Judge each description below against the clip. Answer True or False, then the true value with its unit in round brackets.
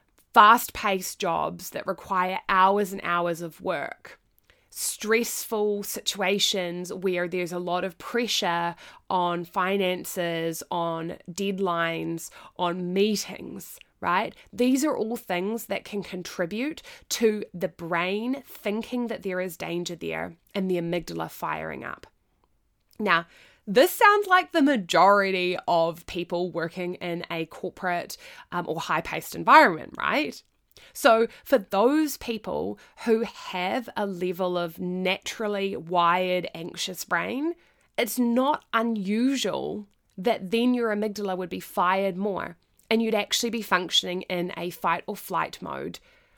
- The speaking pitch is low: False (190 Hz)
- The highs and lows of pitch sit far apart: False (4.2 semitones)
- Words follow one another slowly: True (125 wpm)